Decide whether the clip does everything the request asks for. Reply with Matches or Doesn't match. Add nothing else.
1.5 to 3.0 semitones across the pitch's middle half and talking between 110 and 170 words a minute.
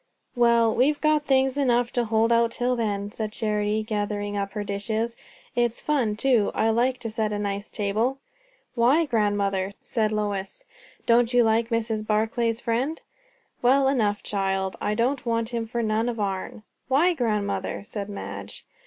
Matches